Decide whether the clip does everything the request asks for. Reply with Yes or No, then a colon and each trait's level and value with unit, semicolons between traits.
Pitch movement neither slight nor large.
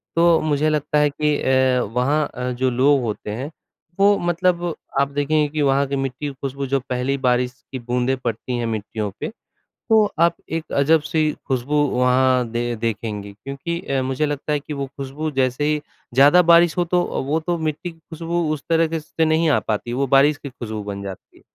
Yes: average, 3.6 semitones